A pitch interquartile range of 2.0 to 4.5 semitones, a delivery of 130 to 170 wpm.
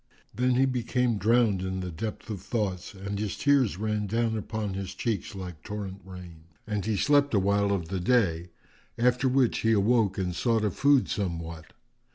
No: average, 3.9 semitones; average, 185 wpm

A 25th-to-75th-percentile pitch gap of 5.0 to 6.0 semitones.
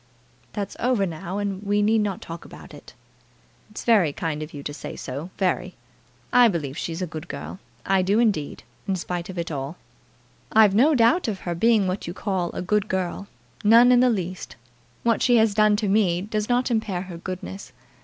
No: average, 3.9 semitones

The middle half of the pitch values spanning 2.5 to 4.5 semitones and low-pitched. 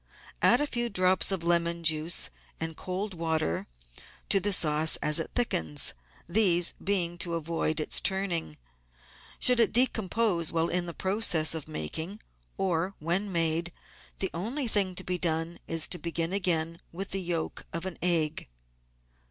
No: average, 2.9 semitones; medium, 175 Hz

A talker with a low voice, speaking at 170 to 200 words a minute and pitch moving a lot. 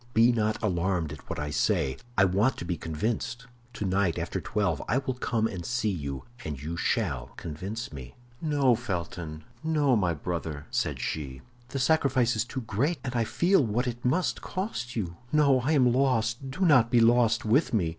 Yes: low, 115 Hz; average, 185 wpm; wide, 6.8 semitones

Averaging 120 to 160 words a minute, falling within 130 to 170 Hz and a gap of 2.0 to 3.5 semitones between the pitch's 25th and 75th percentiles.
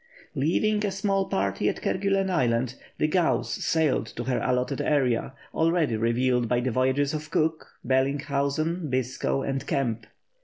No: average, 145 wpm; medium, 140 Hz; average, 4.5 semitones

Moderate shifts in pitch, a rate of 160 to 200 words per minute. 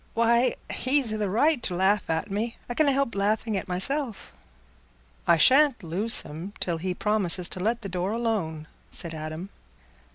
Yes: average, 4.8 semitones; average, 165 wpm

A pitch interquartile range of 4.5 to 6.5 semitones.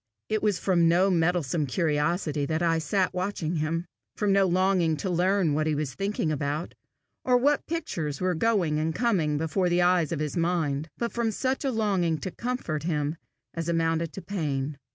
No: average, 4.0 semitones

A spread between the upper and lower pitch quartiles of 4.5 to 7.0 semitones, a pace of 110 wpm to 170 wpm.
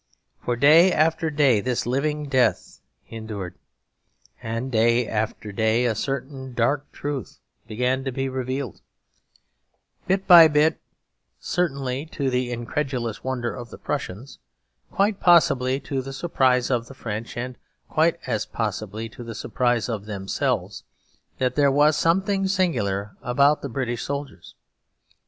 No: average, 3.8 semitones; slow, 135 wpm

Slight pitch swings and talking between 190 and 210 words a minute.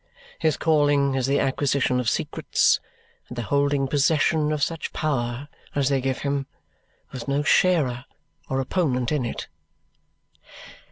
No: narrow, 2.1 semitones; slow, 135 wpm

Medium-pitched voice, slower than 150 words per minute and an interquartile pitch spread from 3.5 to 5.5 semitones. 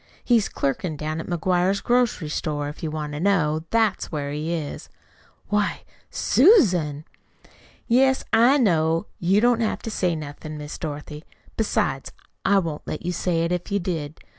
No: medium, 170 Hz; average, 165 wpm; average, 5.2 semitones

